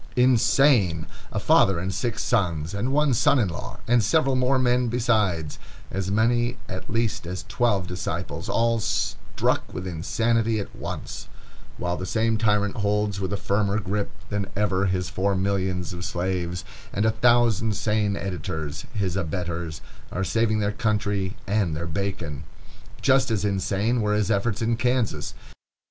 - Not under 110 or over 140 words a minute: No, average, 150 wpm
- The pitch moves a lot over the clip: No, average, 3.7 semitones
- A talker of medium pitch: No, low, 100 Hz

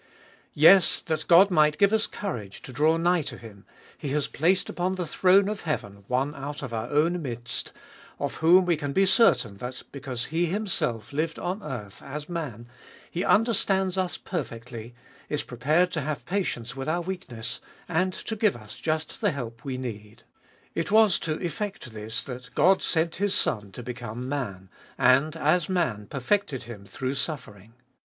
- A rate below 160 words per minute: No, average, 175 wpm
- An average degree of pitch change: No, wide, 6.8 semitones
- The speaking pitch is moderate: Yes, medium, 150 Hz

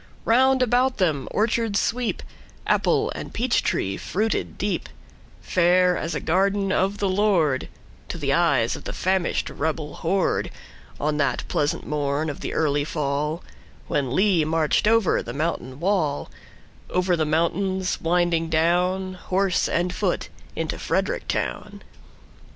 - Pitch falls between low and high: Yes, medium, 175 Hz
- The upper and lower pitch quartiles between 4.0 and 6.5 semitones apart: Yes, average, 4.5 semitones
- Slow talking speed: Yes, slow, 120 wpm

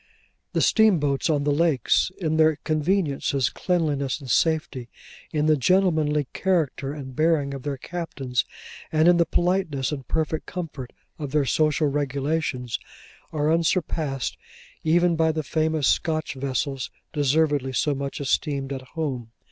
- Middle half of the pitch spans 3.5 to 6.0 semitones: No, average, 2.7 semitones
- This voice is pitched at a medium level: Yes, medium, 150 Hz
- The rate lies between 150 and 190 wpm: No, average, 140 wpm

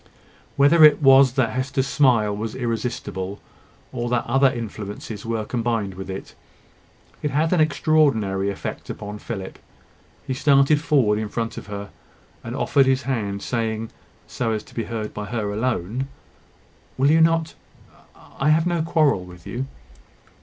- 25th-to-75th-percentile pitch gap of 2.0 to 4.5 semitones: No, average, 4.9 semitones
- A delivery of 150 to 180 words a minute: Yes, average, 155 wpm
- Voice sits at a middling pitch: No, low, 120 Hz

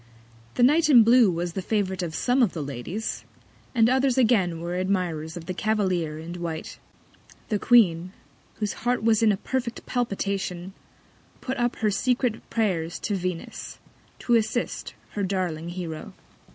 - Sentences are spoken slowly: No, average, 155 wpm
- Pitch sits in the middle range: No, high, 195 Hz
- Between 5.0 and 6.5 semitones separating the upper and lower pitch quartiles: Yes, average, 5.3 semitones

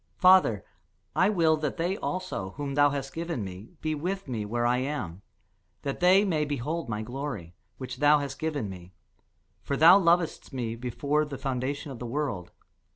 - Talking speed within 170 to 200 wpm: Yes, average, 175 wpm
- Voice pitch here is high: No, medium, 145 Hz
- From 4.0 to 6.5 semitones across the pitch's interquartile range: Yes, average, 5.0 semitones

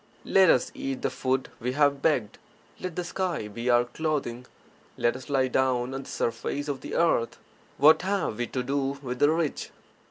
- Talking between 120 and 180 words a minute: No, average, 190 wpm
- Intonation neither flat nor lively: Yes, average, 3.8 semitones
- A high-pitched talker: No, low, 135 Hz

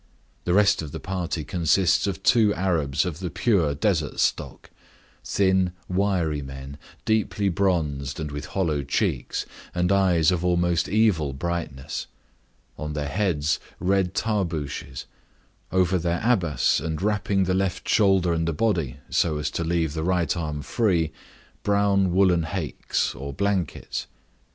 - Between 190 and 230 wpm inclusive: No, average, 140 wpm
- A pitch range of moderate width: Yes, average, 4.1 semitones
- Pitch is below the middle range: Yes, very low, 85 Hz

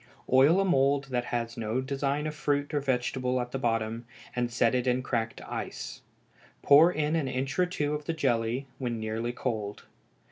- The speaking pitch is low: Yes, low, 130 Hz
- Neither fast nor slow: Yes, average, 185 wpm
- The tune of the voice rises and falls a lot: No, average, 3.3 semitones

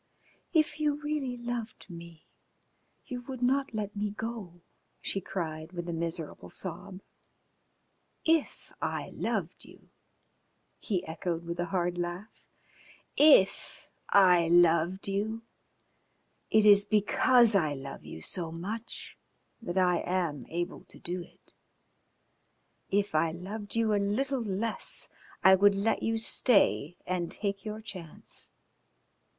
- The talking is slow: Yes, slow, 125 wpm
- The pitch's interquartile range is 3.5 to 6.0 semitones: Yes, average, 4.4 semitones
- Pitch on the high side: Yes, high, 195 Hz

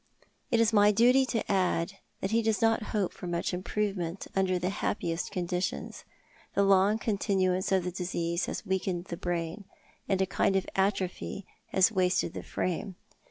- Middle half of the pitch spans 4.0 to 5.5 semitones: No, narrow, 2.4 semitones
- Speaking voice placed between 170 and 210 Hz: Yes, high, 190 Hz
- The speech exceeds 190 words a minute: No, average, 170 wpm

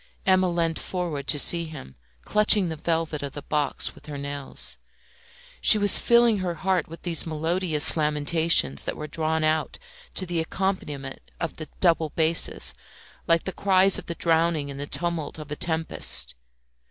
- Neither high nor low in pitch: Yes, medium, 165 Hz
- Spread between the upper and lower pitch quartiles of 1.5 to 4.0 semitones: Yes, average, 2.8 semitones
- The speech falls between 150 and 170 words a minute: Yes, average, 165 wpm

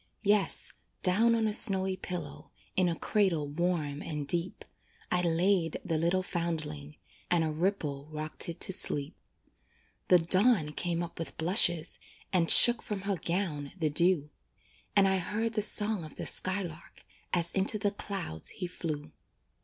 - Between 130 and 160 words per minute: Yes, average, 155 wpm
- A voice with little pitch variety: No, average, 3.7 semitones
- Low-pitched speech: No, medium, 175 Hz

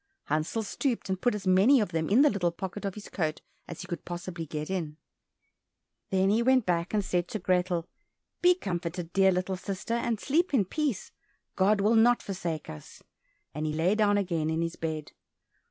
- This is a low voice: No, high, 190 Hz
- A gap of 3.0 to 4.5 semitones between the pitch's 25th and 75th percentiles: Yes, average, 3.9 semitones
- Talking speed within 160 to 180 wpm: No, average, 195 wpm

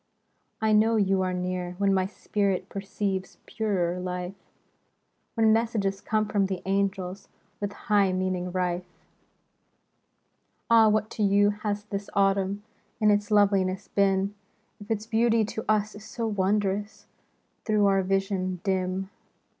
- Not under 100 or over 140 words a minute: Yes, slow, 135 wpm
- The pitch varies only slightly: Yes, narrow, 2.0 semitones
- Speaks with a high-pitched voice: Yes, high, 200 Hz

